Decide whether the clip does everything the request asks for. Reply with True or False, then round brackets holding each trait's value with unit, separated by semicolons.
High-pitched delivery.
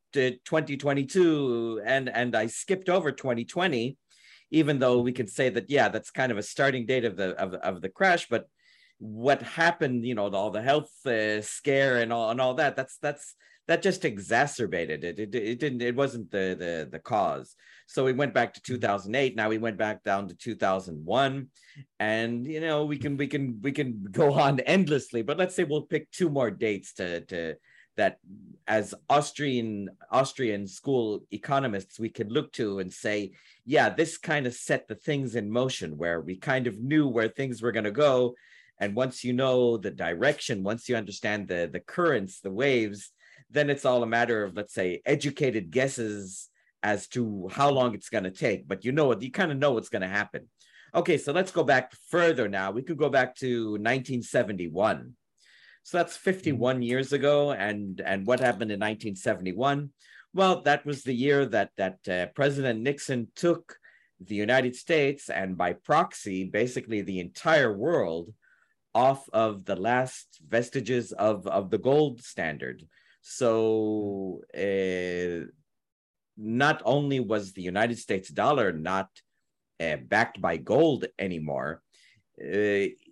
False (125 Hz)